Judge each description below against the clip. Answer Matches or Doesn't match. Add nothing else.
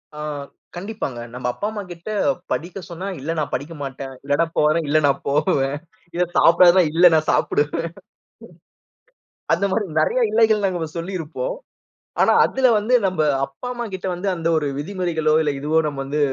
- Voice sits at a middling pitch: Matches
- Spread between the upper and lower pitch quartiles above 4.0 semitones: Matches